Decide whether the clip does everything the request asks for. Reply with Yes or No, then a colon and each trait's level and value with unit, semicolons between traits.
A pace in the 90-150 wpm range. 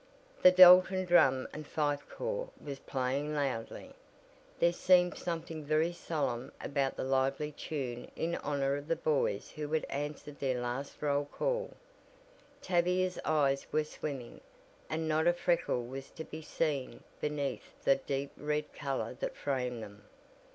Yes: average, 145 wpm